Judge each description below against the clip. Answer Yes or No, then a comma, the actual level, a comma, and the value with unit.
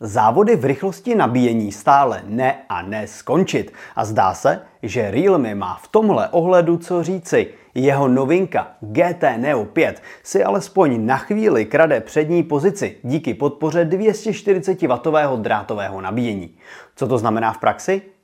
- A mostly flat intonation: No, wide, 7.1 semitones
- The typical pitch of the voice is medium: Yes, medium, 155 Hz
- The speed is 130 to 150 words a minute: Yes, average, 140 wpm